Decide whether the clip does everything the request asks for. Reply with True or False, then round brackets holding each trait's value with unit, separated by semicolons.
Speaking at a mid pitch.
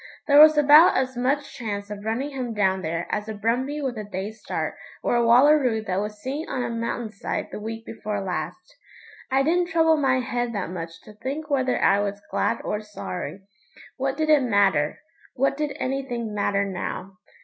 False (235 Hz)